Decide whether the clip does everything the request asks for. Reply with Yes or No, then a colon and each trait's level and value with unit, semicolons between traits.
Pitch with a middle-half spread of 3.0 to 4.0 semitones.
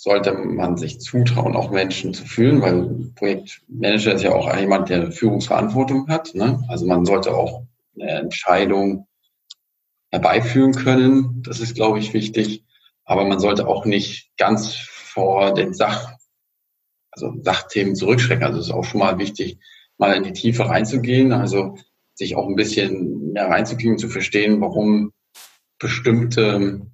Yes: average, 3.7 semitones